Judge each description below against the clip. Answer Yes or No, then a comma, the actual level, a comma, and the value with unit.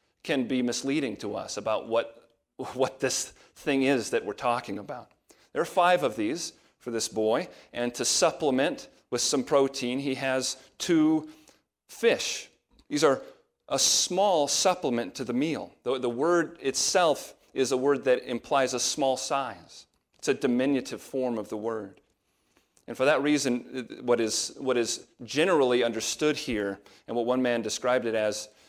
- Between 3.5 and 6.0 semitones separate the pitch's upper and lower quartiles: No, average, 2.9 semitones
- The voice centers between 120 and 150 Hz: Yes, low, 130 Hz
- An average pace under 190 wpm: Yes, average, 165 wpm